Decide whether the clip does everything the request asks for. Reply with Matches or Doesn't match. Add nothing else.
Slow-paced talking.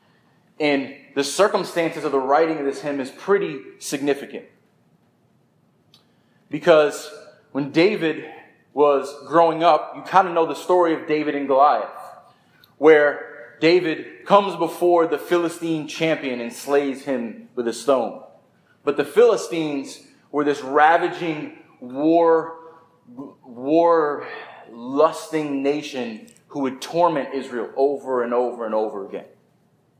Matches